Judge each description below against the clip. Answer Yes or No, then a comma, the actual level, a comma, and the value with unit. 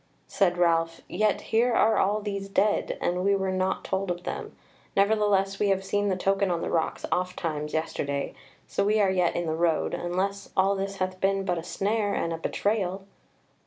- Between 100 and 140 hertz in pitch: No, high, 190 Hz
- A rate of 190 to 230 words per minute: Yes, average, 200 wpm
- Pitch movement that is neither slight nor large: No, narrow, 2.2 semitones